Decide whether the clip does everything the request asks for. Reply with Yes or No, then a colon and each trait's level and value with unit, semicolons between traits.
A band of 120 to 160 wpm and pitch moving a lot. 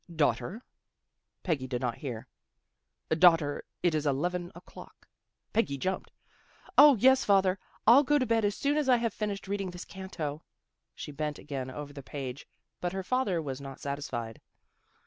No: average, 170 wpm; wide, 6.3 semitones